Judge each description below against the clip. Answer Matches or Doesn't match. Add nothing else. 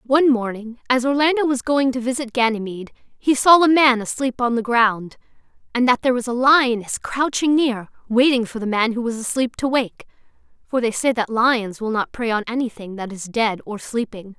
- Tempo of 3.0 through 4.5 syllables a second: Doesn't match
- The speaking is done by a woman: Matches